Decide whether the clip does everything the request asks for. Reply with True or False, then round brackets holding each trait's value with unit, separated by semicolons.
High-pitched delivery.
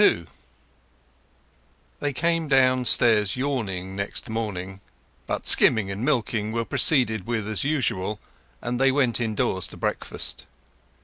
False (115 Hz)